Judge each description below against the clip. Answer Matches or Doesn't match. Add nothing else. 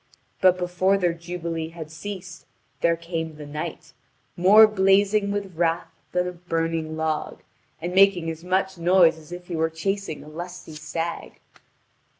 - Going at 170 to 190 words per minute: Doesn't match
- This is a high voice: Doesn't match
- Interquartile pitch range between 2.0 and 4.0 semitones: Matches